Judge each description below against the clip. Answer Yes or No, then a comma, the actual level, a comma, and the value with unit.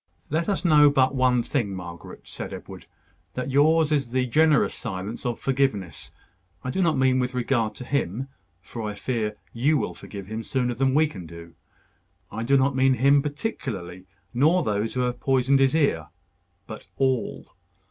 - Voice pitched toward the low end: Yes, low, 130 Hz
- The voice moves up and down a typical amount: Yes, average, 4.2 semitones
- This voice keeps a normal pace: Yes, average, 175 wpm